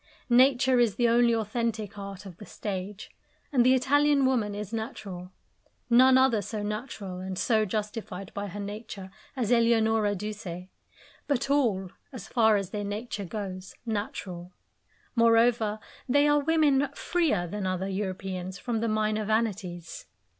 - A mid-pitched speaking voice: No, high, 215 Hz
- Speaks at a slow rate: No, average, 145 wpm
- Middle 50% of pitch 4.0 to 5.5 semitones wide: No, average, 3.5 semitones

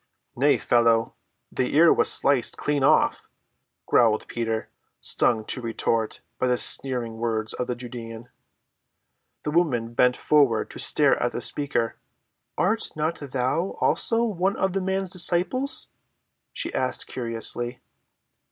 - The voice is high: No, low, 125 Hz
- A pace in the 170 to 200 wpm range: No, slow, 135 wpm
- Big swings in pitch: Yes, wide, 6.4 semitones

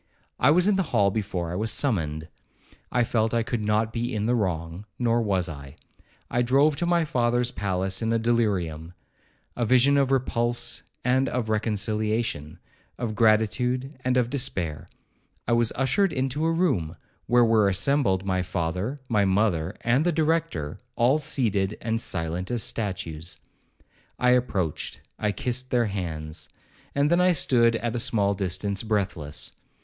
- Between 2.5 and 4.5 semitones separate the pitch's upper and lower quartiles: No, average, 5.0 semitones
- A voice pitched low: Yes, low, 110 Hz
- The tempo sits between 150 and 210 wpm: Yes, average, 155 wpm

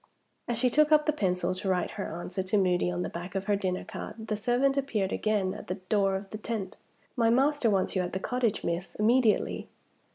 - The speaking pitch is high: Yes, high, 205 Hz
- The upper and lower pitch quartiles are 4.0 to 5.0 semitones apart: Yes, average, 4.3 semitones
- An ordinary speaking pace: No, fast, 225 wpm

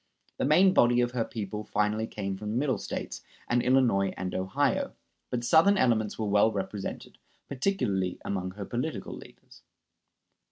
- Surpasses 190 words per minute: No, average, 155 wpm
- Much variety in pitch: No, average, 4.2 semitones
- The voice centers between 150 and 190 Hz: No, low, 110 Hz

